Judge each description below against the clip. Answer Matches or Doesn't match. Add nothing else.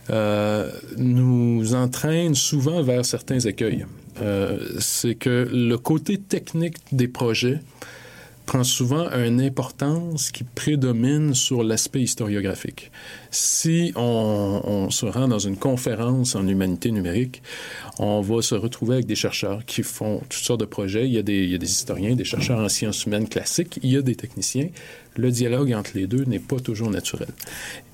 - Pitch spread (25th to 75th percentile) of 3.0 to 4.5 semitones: Matches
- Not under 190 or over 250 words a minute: Doesn't match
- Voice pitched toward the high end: Doesn't match